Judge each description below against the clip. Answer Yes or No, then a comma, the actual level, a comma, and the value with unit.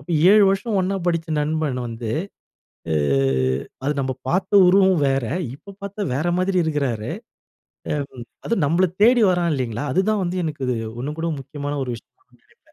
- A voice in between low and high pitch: Yes, medium, 160 Hz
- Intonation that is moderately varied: No, wide, 5.8 semitones